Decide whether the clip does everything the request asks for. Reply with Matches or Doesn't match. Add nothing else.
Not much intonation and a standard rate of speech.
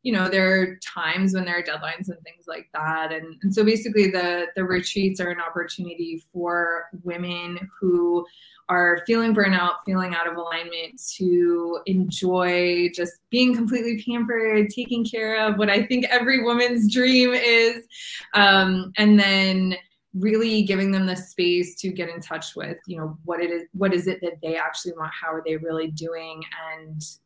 Doesn't match